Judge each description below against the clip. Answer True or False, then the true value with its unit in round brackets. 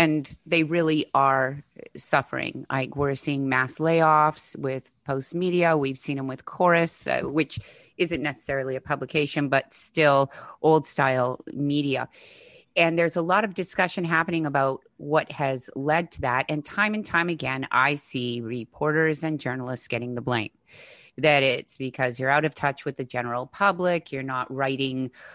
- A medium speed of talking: True (165 wpm)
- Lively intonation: False (3.6 semitones)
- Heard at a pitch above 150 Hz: False (145 Hz)